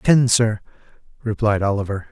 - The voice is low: Yes, low, 110 Hz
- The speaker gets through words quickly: No, slow, 115 wpm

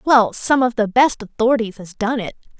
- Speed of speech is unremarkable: No, fast, 210 wpm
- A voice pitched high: Yes, high, 230 Hz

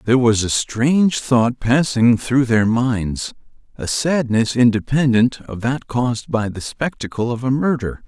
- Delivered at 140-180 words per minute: Yes, average, 155 wpm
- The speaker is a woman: No, male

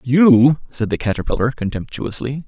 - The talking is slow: Yes, slow, 120 wpm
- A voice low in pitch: Yes, low, 130 Hz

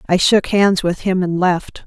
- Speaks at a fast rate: Yes, fast, 225 wpm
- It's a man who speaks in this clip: No, female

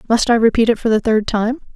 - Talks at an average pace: No, fast, 275 wpm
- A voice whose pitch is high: Yes, high, 225 Hz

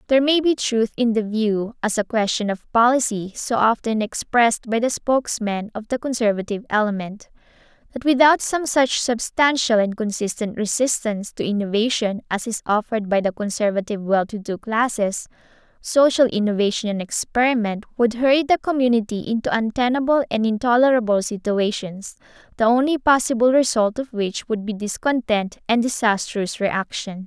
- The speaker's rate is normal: Yes, average, 145 wpm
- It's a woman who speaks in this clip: Yes, female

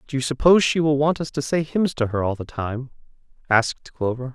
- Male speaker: Yes, male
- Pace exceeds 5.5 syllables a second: Yes, 5.8 syllables/s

